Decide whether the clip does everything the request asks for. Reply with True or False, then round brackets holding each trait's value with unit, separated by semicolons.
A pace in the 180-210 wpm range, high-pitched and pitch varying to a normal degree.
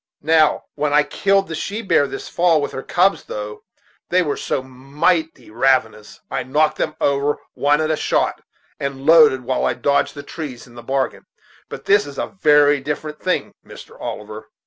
False (185 wpm; 145 Hz; 3.0 semitones)